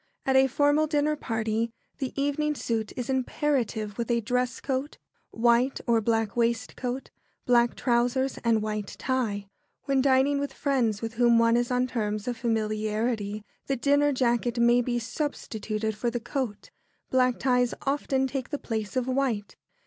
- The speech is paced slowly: No, average, 155 wpm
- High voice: Yes, high, 245 Hz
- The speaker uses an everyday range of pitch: Yes, average, 3.0 semitones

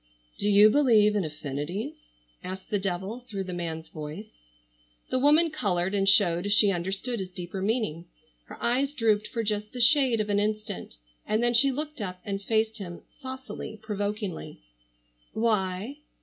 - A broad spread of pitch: No, average, 3.8 semitones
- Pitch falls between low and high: No, high, 210 Hz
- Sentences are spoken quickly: No, average, 160 wpm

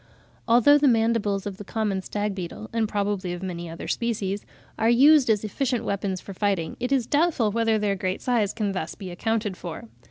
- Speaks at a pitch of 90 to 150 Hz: No, high, 210 Hz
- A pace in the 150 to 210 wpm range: Yes, average, 195 wpm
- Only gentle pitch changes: No, average, 3.3 semitones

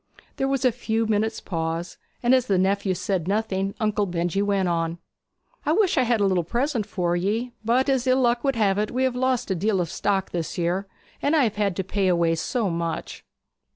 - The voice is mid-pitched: No, high, 205 Hz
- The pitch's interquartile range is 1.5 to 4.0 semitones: No, average, 5.0 semitones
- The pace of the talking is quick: Yes, fast, 220 wpm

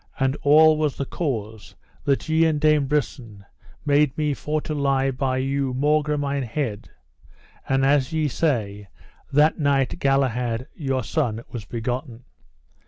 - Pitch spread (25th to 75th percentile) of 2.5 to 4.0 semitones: Yes, average, 3.0 semitones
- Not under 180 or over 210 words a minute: No, average, 145 wpm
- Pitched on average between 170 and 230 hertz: No, low, 135 Hz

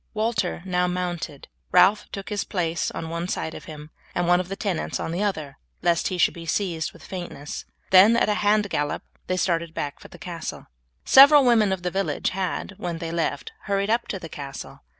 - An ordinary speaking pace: No, fast, 210 wpm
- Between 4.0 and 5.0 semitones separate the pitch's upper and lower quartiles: No, average, 3.2 semitones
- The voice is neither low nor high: Yes, medium, 180 Hz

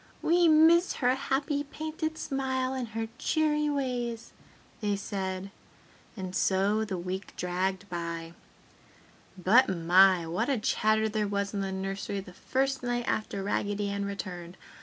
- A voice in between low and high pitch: No, high, 205 Hz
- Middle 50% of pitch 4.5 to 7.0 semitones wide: Yes, wide, 5.6 semitones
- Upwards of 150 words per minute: No, average, 140 wpm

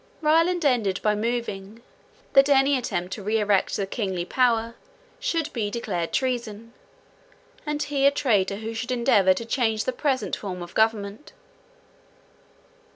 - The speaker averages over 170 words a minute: No, average, 145 wpm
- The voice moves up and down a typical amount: Yes, average, 4.5 semitones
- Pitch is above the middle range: Yes, high, 230 Hz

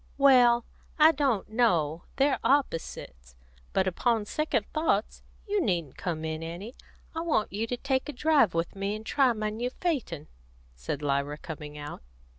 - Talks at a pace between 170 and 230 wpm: No, average, 160 wpm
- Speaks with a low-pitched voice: No, high, 215 Hz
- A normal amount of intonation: No, wide, 8.6 semitones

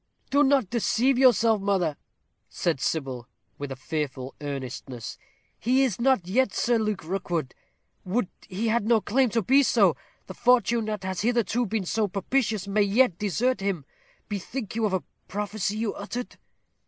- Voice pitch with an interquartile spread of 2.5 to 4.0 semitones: No, average, 4.8 semitones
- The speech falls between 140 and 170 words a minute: Yes, average, 160 wpm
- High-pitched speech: Yes, high, 210 Hz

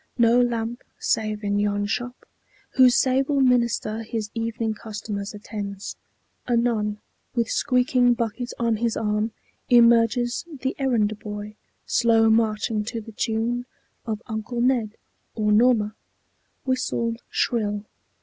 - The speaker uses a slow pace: Yes, slow, 120 wpm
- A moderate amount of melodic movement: No, narrow, 2.3 semitones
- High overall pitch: Yes, high, 225 Hz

